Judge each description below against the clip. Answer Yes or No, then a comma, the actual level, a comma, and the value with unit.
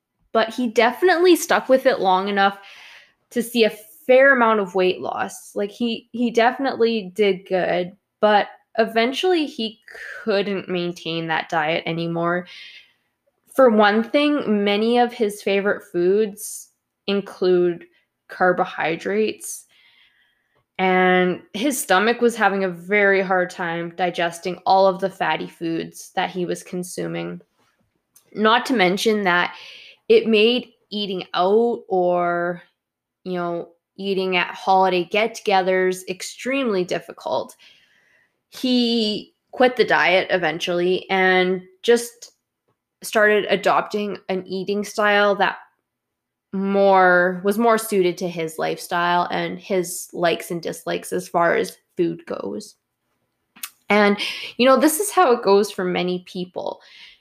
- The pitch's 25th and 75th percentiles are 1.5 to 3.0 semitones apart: No, average, 3.8 semitones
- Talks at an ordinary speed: No, slow, 125 wpm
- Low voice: No, high, 195 Hz